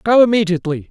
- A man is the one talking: Yes, male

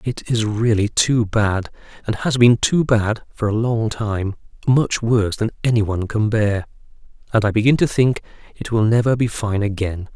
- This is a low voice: Yes, low, 110 Hz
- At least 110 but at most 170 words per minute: No, average, 190 wpm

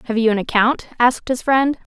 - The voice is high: Yes, high, 240 Hz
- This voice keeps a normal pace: No, fast, 215 wpm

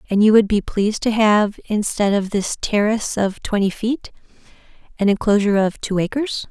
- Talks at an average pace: Yes, average, 175 wpm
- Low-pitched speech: No, high, 210 Hz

